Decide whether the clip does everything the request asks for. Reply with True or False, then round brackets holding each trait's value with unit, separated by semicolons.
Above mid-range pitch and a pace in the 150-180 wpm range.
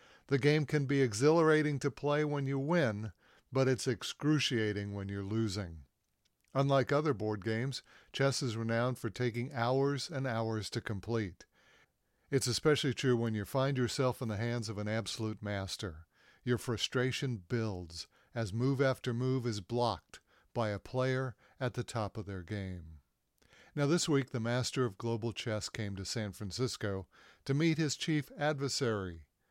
False (120 Hz; 160 wpm)